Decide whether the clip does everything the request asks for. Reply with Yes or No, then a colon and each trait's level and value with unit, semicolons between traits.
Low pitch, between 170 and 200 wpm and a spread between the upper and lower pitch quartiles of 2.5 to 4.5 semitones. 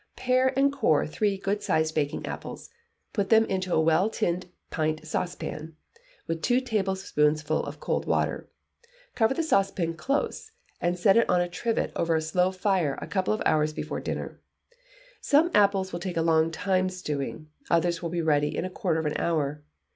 No: medium, 180 Hz; average, 180 wpm; average, 4.1 semitones